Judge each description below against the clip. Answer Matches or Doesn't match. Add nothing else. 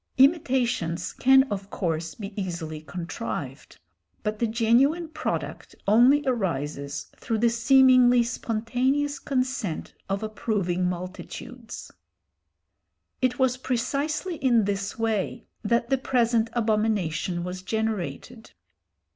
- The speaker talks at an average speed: Doesn't match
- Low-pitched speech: Doesn't match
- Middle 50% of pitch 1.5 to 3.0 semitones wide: Doesn't match